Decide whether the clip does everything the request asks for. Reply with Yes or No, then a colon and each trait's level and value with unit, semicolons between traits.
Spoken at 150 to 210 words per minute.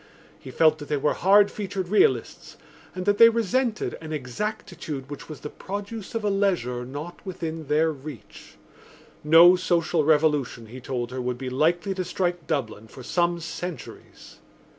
Yes: average, 160 wpm